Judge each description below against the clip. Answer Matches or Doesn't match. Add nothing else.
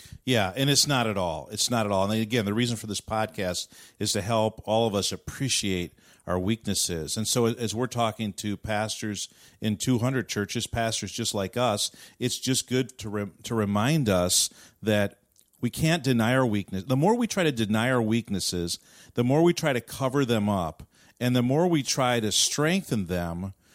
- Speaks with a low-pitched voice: Matches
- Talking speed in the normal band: Matches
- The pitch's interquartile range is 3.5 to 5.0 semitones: Matches